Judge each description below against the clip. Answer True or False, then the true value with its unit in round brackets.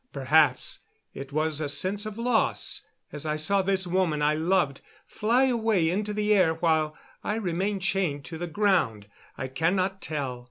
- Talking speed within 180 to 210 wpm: False (165 wpm)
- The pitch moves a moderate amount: True (4.7 semitones)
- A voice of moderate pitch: True (175 Hz)